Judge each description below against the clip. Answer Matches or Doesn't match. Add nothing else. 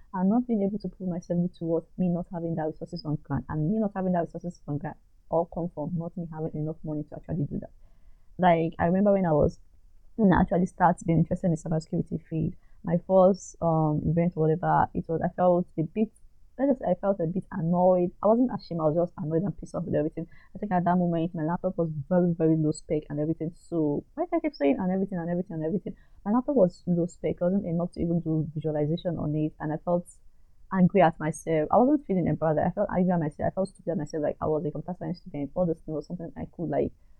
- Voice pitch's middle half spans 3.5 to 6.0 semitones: Doesn't match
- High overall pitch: Doesn't match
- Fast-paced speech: Matches